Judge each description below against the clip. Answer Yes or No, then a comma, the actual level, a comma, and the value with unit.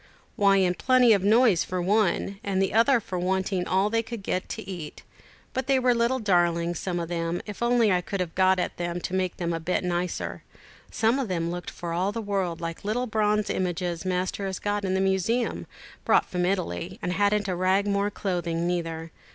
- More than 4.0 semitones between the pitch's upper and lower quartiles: No, average, 3.0 semitones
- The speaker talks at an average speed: No, fast, 215 wpm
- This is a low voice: No, high, 190 Hz